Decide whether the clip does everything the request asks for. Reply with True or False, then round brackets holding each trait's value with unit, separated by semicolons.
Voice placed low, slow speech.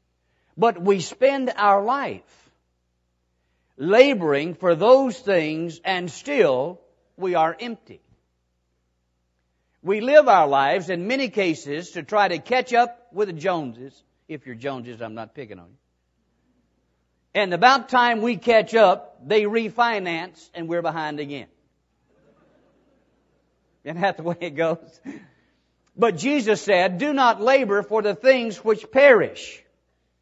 False (175 Hz; 130 wpm)